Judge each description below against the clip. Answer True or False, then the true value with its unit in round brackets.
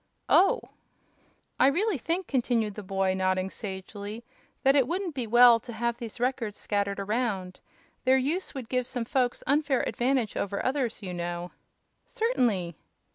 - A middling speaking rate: True (150 wpm)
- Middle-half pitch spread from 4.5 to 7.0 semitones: True (4.9 semitones)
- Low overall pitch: False (235 Hz)